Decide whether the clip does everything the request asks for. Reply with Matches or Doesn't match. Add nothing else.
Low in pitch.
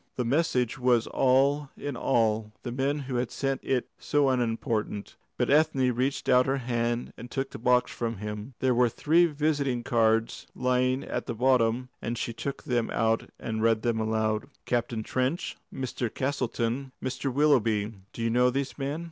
Matches